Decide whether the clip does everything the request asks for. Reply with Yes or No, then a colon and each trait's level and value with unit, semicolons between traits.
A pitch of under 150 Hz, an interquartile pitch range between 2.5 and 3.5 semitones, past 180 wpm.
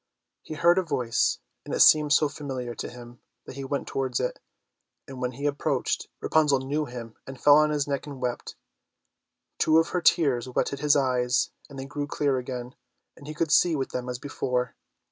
Yes: low, 135 Hz; average, 2.8 semitones; average, 200 wpm